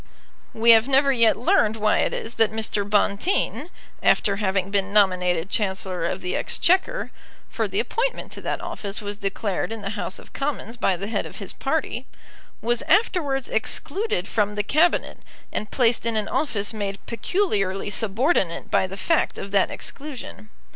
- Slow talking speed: No, average, 170 wpm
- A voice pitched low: No, high, 215 Hz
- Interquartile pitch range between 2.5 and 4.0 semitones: No, average, 4.8 semitones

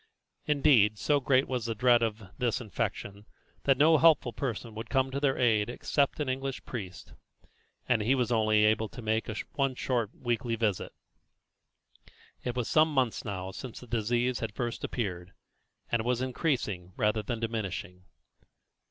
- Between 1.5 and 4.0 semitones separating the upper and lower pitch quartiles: Yes, average, 3.4 semitones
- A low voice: Yes, low, 120 Hz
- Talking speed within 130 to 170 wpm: Yes, average, 160 wpm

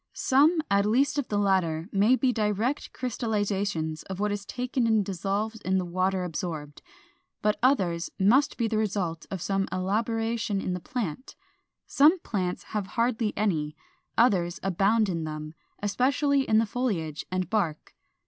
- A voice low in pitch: No, high, 205 Hz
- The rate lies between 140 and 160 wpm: Yes, average, 155 wpm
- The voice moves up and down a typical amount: Yes, average, 4.1 semitones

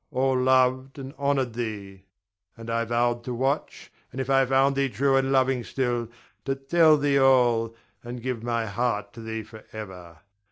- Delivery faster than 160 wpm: Yes, average, 170 wpm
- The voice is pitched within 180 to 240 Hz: No, low, 125 Hz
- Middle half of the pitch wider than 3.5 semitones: No, average, 2.7 semitones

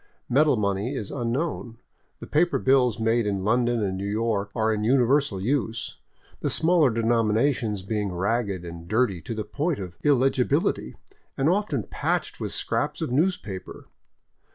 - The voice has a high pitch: No, low, 115 Hz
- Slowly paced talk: No, average, 155 wpm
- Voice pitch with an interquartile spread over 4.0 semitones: Yes, average, 4.7 semitones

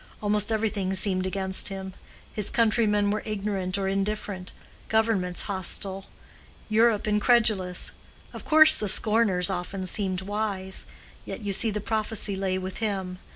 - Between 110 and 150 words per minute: Yes, slow, 135 wpm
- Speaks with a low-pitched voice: No, high, 200 Hz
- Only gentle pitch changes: Yes, narrow, 2.2 semitones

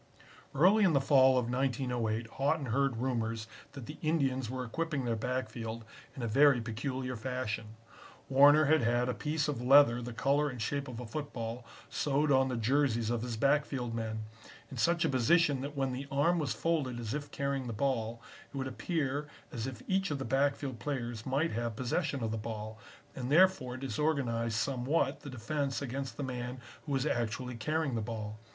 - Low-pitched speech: Yes, low, 130 Hz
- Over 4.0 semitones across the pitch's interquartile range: No, average, 3.4 semitones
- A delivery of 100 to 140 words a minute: No, average, 185 wpm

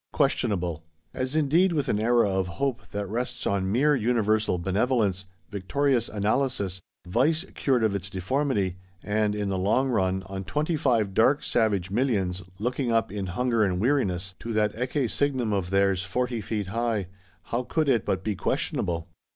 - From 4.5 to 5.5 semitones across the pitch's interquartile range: Yes, average, 4.8 semitones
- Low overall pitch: Yes, low, 110 Hz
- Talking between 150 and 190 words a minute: Yes, average, 160 wpm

